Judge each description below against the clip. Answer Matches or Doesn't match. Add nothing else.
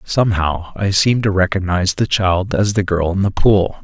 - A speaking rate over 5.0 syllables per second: Matches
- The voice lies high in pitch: Doesn't match